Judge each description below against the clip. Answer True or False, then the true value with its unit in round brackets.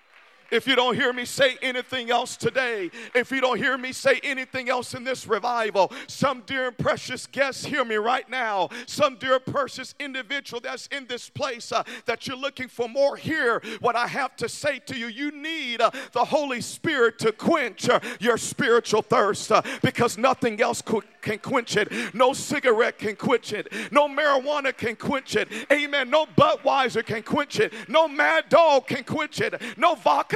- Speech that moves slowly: False (190 wpm)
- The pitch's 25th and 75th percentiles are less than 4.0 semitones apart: True (2.8 semitones)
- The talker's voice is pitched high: True (255 Hz)